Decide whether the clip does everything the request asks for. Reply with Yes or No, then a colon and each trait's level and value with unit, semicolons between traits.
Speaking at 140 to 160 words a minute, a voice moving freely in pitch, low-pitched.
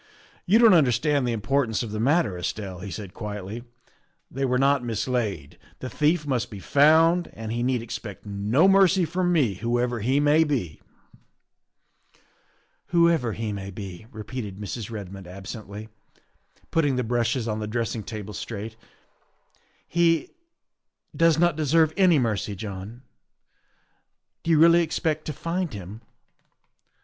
Yes: average, 150 wpm; wide, 6.8 semitones; low, 120 Hz